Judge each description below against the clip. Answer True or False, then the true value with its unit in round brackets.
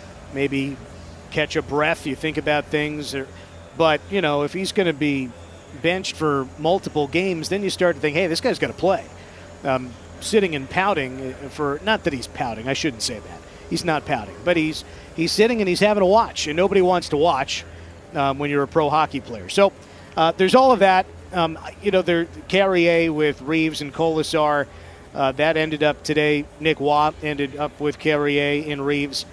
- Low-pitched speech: False (150 Hz)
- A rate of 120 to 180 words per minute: False (200 wpm)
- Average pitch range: True (3.7 semitones)